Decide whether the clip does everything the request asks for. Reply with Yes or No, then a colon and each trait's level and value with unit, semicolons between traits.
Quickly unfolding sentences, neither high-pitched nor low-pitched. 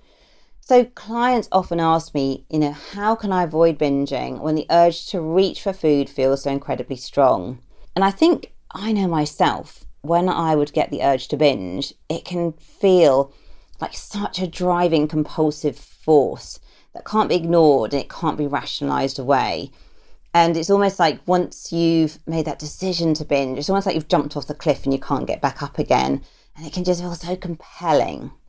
No: average, 185 wpm; medium, 165 Hz